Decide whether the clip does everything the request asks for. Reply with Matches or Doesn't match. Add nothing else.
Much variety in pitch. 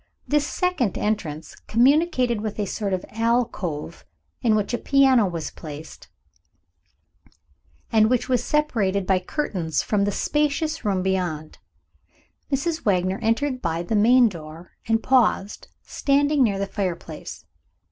Matches